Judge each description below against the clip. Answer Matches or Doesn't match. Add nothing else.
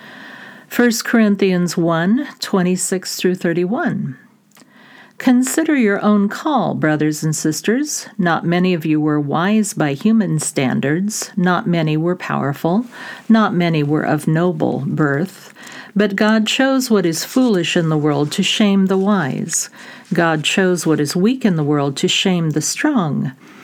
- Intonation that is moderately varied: Doesn't match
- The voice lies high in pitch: Matches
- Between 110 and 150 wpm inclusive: Matches